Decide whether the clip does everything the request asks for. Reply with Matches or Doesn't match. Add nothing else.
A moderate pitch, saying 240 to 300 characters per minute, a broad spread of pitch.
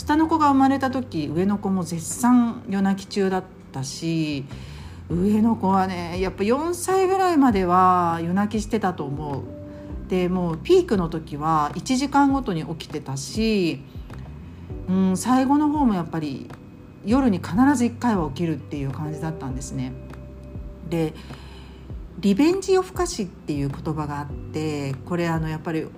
Matches